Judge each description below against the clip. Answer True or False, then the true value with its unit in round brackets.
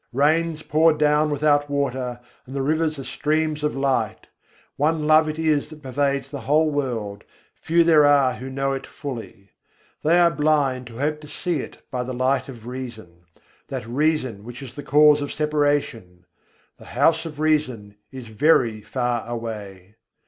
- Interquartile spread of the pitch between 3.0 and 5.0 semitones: True (3.7 semitones)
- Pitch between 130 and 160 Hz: True (140 Hz)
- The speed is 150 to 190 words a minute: True (170 wpm)